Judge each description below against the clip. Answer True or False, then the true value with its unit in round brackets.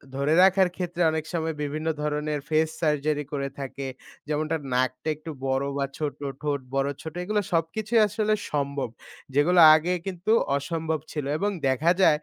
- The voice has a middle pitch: True (155 Hz)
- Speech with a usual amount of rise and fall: True (3.2 semitones)